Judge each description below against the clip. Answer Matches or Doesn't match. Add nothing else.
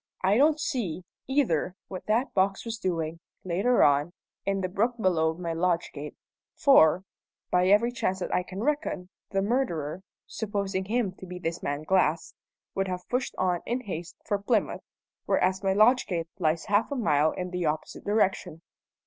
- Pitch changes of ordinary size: Matches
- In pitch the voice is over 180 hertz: Matches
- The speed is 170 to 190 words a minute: Matches